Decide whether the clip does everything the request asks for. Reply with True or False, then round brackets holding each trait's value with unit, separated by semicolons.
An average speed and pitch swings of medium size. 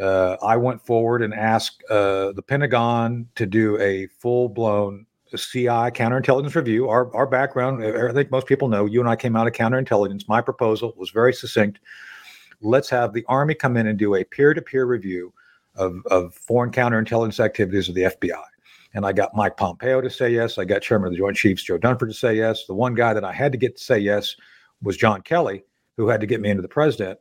False (220 wpm; 3.5 semitones)